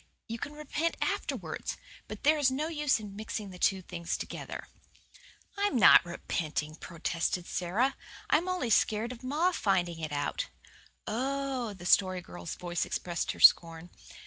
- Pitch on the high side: Yes, high, 210 Hz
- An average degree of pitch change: No, wide, 7.9 semitones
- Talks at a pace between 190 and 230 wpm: No, average, 150 wpm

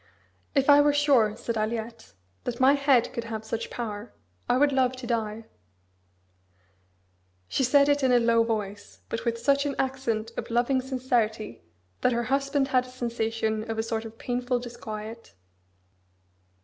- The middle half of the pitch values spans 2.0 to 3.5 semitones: Yes, average, 2.8 semitones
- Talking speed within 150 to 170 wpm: Yes, average, 160 wpm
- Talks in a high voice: Yes, high, 240 Hz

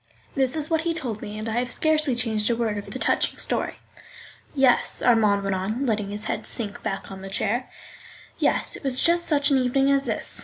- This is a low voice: No, high, 240 Hz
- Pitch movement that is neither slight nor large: Yes, average, 4.7 semitones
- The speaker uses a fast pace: Yes, fast, 220 wpm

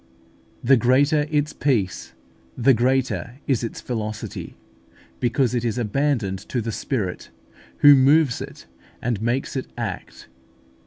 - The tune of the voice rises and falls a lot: No, average, 3.2 semitones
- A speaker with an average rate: No, slow, 125 wpm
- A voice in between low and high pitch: No, low, 125 Hz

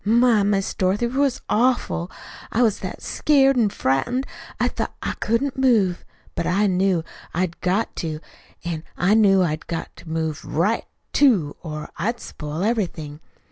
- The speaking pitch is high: Yes, high, 195 Hz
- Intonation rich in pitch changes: Yes, wide, 6.0 semitones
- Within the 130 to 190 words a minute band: Yes, average, 155 wpm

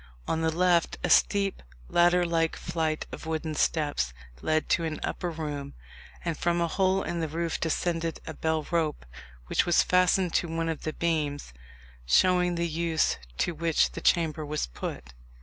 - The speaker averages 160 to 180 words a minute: Yes, average, 170 wpm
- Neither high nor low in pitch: Yes, medium, 165 Hz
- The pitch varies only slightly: Yes, narrow, 1.8 semitones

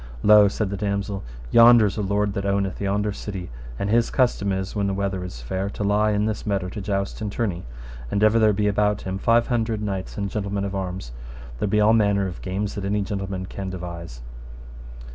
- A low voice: Yes, low, 100 Hz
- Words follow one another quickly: Yes, fast, 220 wpm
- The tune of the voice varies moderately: No, narrow, 1.6 semitones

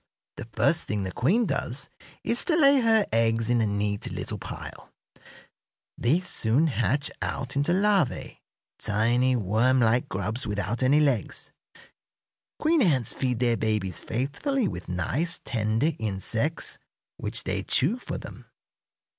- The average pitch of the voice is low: Yes, low, 125 Hz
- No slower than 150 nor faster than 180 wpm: No, average, 140 wpm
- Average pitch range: No, wide, 6.8 semitones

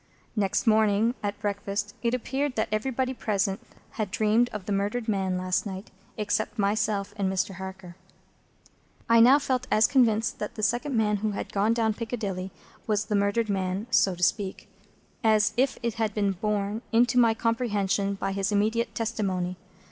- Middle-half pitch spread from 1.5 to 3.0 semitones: Yes, narrow, 2.4 semitones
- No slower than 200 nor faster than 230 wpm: No, average, 170 wpm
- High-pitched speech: Yes, high, 210 Hz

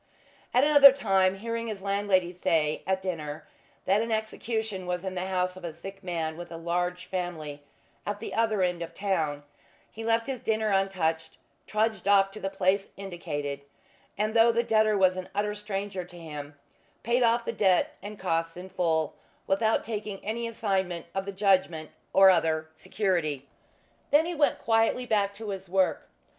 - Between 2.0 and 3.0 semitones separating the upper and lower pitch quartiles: No, average, 3.7 semitones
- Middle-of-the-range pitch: No, high, 195 Hz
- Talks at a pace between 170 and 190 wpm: Yes, average, 175 wpm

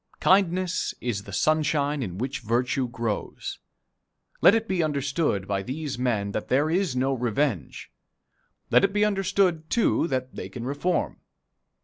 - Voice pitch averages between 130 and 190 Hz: Yes, medium, 140 Hz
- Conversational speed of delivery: Yes, average, 145 wpm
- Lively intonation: Yes, wide, 6.3 semitones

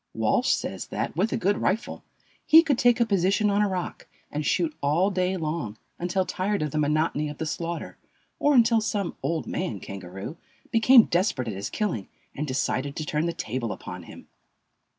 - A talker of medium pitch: Yes, medium, 170 Hz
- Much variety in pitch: Yes, wide, 6.0 semitones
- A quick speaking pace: No, average, 190 wpm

